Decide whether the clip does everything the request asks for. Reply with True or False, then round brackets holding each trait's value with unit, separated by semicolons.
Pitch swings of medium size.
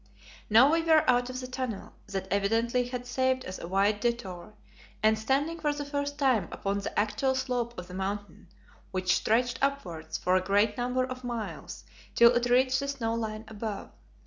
True (4.1 semitones)